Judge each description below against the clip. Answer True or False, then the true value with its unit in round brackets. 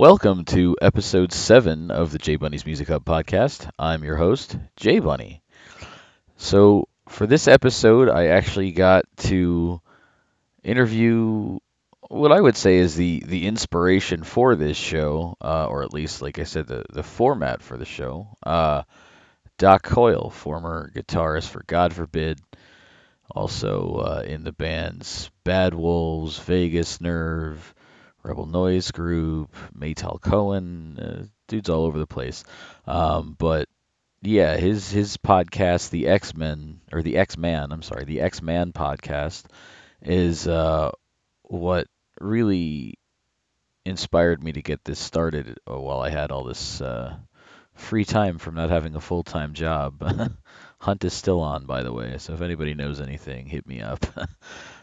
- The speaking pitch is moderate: False (85 Hz)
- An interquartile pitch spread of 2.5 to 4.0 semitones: True (3.2 semitones)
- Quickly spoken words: False (150 wpm)